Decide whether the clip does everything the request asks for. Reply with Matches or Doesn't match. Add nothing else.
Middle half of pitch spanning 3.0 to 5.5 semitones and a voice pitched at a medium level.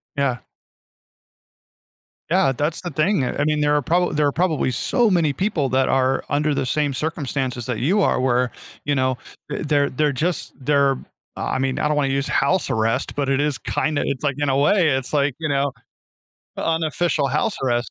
Doesn't match